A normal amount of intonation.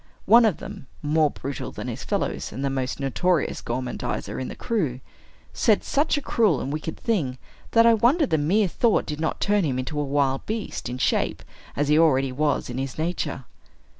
No: wide, 7.3 semitones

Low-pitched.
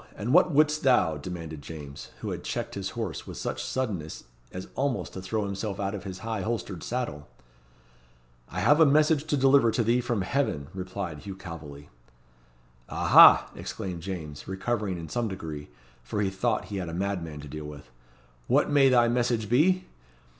Yes: low, 100 Hz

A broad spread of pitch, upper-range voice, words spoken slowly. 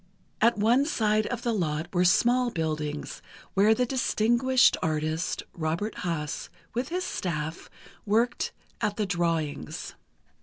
Yes: wide, 6.8 semitones; high, 205 Hz; slow, 125 wpm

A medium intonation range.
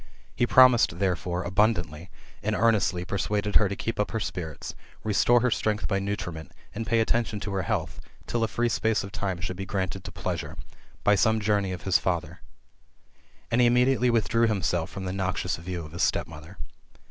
Yes: average, 3.7 semitones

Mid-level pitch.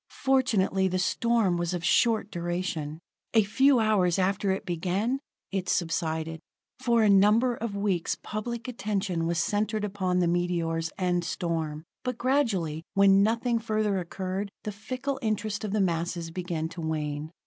No: high, 195 Hz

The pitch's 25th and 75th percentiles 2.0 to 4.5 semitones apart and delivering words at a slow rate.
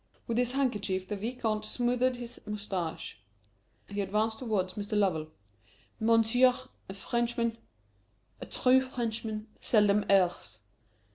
Yes: average, 3.2 semitones; slow, 115 wpm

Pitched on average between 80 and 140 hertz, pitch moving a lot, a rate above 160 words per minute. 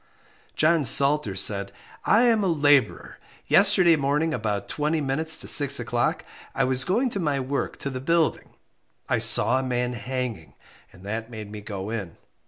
Yes: low, 135 Hz; wide, 5.8 semitones; average, 170 wpm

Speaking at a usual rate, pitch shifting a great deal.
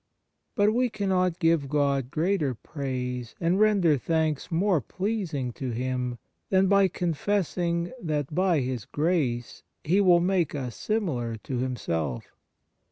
No: slow, 130 wpm; wide, 6.4 semitones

